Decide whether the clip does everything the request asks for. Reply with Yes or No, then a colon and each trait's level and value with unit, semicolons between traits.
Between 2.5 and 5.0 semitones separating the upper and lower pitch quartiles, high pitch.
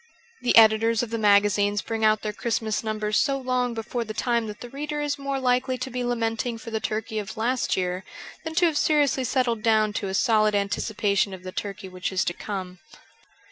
Yes: average, 3.1 semitones; high, 225 Hz